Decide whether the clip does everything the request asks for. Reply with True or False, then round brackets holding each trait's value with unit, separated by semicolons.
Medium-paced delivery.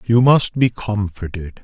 True (145 wpm)